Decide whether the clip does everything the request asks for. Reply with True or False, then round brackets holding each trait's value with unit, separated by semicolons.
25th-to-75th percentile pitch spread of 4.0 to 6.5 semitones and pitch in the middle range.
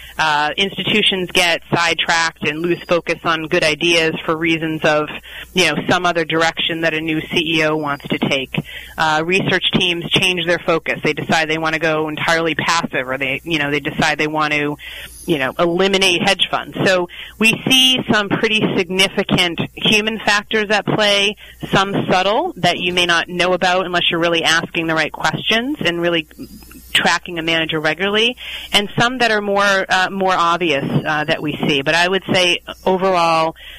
False (3.2 semitones; 170 Hz)